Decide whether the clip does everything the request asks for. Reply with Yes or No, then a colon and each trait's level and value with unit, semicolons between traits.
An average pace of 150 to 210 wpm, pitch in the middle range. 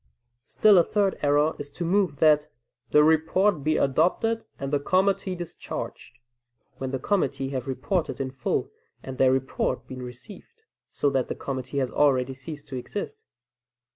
Yes: average, 160 wpm; medium, 145 Hz